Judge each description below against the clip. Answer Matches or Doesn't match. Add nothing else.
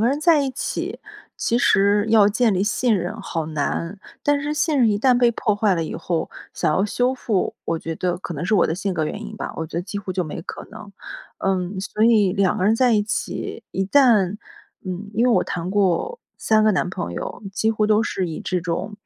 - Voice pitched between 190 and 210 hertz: Matches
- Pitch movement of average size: Matches